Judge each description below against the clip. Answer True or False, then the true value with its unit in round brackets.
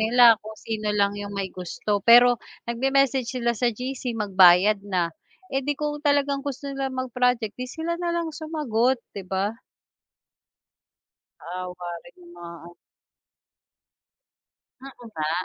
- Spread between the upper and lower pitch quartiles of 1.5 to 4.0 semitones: False (5.2 semitones)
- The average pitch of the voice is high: True (235 Hz)